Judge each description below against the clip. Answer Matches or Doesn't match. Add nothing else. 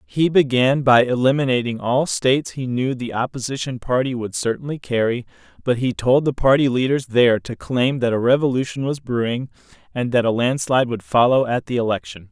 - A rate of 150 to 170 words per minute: Doesn't match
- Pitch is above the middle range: Doesn't match